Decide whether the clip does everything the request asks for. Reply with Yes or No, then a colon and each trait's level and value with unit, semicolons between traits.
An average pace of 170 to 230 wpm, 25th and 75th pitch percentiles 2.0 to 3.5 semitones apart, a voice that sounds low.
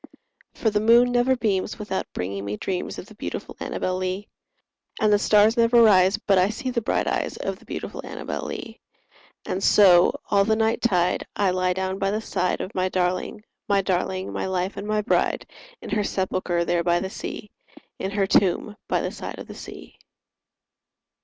No: average, 190 wpm; narrow, 2.6 semitones; high, 195 Hz